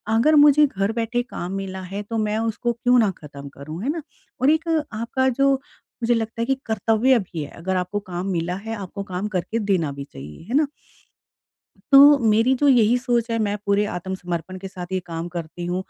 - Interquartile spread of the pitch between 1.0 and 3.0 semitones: No, average, 4.9 semitones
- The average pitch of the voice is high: Yes, high, 210 Hz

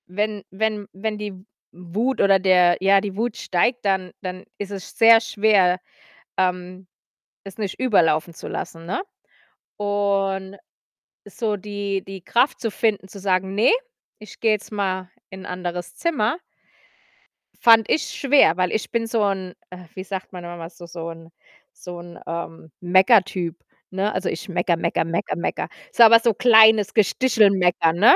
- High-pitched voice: Yes, high, 195 Hz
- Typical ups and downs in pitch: Yes, average, 3.0 semitones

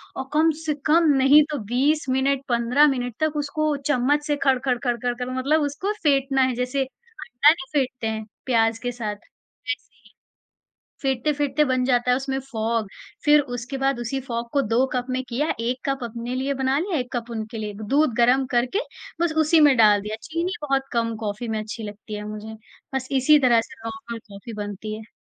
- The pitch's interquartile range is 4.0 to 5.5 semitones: No, average, 3.5 semitones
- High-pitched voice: Yes, very high, 255 Hz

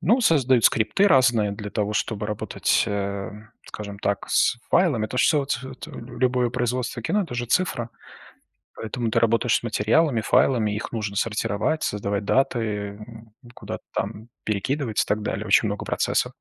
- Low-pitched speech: Yes, low, 115 Hz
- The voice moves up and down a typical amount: Yes, average, 3.2 semitones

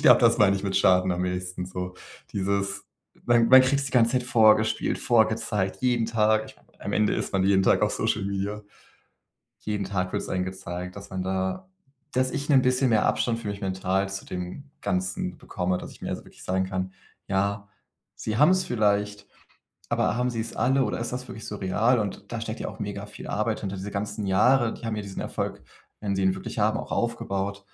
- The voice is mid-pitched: No, low, 100 Hz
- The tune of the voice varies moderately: Yes, average, 3.4 semitones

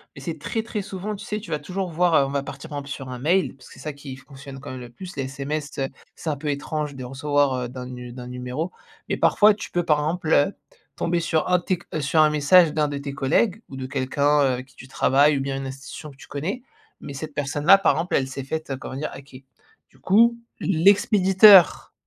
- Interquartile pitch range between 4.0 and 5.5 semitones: Yes, average, 4.4 semitones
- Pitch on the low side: No, medium, 145 Hz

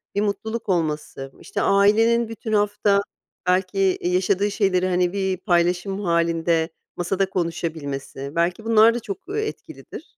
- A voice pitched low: No, high, 190 Hz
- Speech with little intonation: No, average, 3.3 semitones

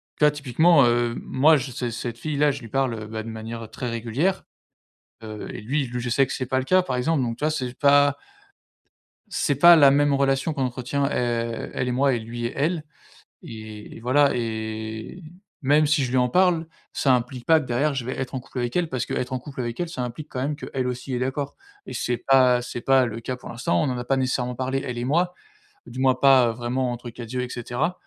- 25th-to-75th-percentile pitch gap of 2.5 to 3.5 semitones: Yes, average, 2.9 semitones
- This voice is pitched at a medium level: No, low, 130 Hz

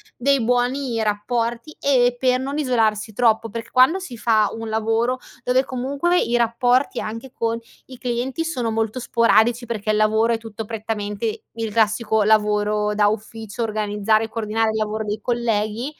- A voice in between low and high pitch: No, high, 225 Hz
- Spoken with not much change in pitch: Yes, narrow, 2.3 semitones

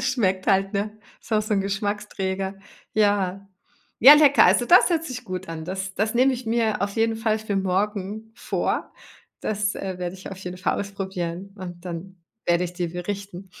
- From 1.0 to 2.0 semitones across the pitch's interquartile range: No, average, 2.7 semitones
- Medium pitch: No, high, 195 Hz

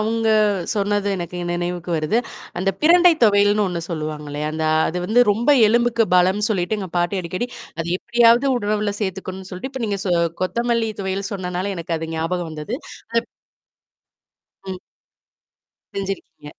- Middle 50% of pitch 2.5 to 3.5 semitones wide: No, average, 4.0 semitones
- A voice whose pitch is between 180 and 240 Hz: Yes, high, 195 Hz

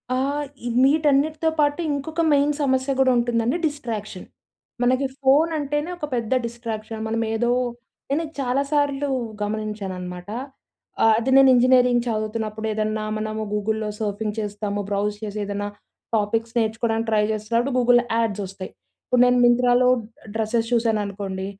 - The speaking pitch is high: Yes, high, 230 Hz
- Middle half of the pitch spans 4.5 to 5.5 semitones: No, average, 3.5 semitones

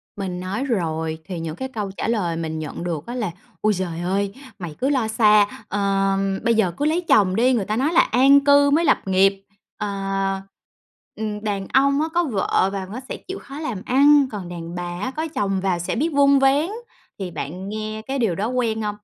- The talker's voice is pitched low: No, high, 205 Hz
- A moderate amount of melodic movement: No, wide, 5.7 semitones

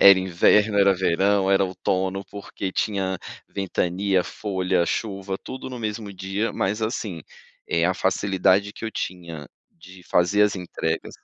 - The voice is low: Yes, very low, 95 Hz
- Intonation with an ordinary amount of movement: No, narrow, 1.8 semitones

